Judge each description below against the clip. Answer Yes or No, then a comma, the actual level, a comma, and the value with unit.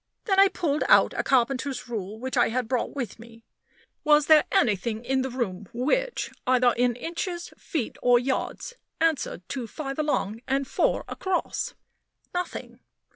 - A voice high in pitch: Yes, very high, 260 Hz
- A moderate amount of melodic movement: Yes, average, 4.5 semitones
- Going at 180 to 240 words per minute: No, average, 155 wpm